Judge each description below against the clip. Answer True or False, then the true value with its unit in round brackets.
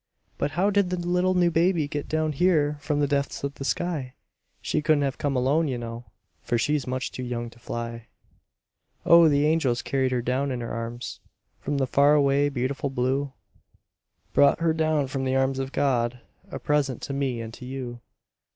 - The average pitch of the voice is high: False (140 Hz)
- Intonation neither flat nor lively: True (3.2 semitones)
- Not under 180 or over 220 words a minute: True (195 wpm)